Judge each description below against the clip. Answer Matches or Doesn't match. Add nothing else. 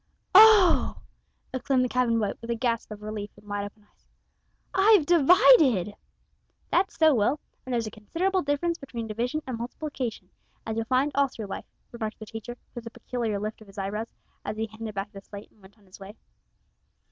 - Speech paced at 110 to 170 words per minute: Doesn't match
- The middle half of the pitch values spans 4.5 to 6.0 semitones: Matches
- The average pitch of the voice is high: Matches